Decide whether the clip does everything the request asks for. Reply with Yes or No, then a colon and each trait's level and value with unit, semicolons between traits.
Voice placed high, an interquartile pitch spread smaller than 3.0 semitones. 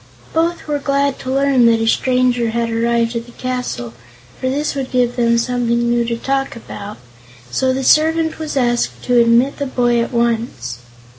Yes: high, 245 Hz; narrow, 2.6 semitones